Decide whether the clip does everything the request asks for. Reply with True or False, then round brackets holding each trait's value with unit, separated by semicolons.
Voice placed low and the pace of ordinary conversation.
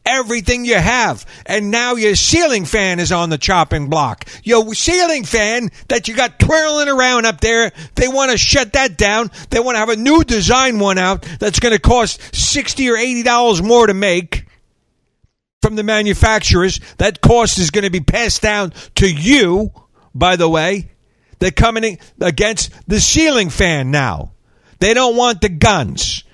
False (215 Hz; 180 wpm)